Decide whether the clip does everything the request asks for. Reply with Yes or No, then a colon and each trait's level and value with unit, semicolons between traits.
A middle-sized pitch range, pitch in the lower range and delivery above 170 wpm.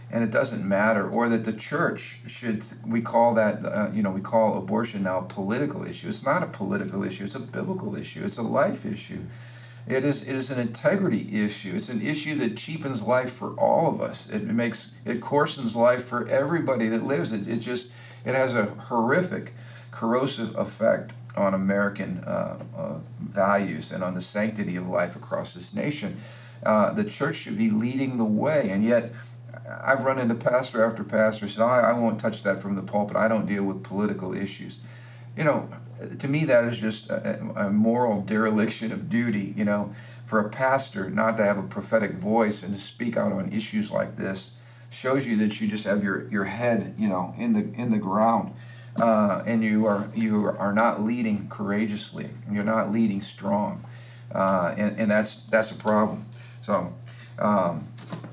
No: narrow, 2.3 semitones; low, 115 Hz; average, 190 wpm